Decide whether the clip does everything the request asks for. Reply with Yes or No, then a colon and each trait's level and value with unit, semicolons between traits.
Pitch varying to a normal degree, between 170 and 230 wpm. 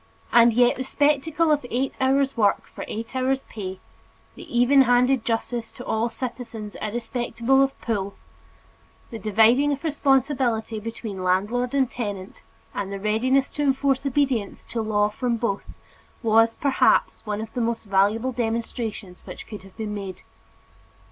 No: average, 3.6 semitones; average, 150 wpm